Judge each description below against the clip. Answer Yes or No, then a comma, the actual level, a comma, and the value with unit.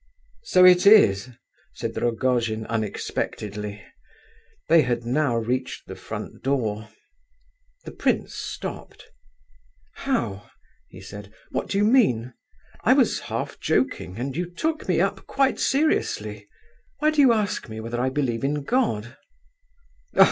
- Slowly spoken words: Yes, slow, 130 wpm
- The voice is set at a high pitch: No, low, 130 Hz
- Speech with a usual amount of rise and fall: No, wide, 8.9 semitones